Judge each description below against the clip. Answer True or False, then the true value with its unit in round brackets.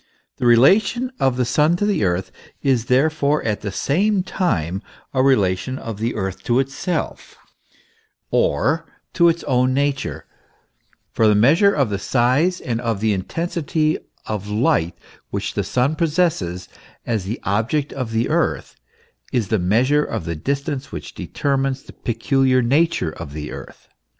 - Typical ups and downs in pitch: False (6.1 semitones)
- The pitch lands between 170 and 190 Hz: False (130 Hz)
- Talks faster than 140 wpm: True (155 wpm)